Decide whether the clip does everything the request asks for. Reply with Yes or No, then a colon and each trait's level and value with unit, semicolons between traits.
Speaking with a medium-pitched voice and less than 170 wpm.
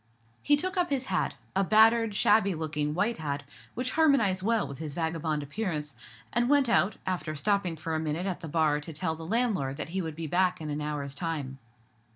No: medium, 165 Hz; average, 195 wpm